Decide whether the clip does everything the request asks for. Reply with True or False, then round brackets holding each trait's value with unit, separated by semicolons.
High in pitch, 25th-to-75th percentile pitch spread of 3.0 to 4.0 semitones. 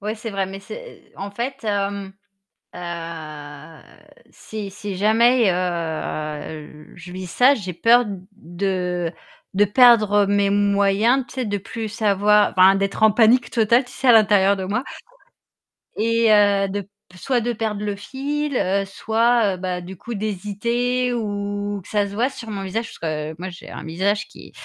True (205 Hz; 3.4 semitones)